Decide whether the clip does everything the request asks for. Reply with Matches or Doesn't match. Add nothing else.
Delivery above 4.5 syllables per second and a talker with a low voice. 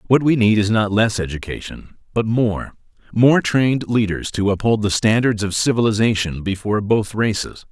Matches